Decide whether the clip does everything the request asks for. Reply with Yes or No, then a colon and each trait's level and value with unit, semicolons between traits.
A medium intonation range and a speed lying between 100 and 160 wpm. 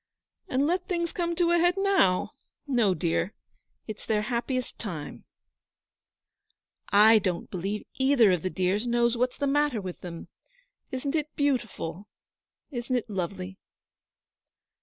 No: wide, 7.2 semitones; slow, 135 wpm